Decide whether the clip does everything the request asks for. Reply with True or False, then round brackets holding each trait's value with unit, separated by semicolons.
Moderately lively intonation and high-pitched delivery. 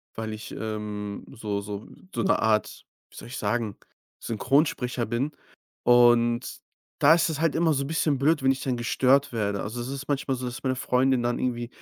False (3.7 semitones; 120 Hz)